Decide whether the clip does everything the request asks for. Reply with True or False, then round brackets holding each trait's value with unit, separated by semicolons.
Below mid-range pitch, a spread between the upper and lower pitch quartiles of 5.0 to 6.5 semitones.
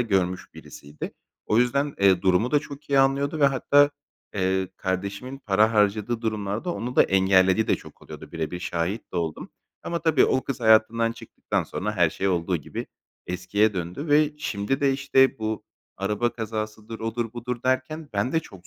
True (110 Hz; 5.6 semitones)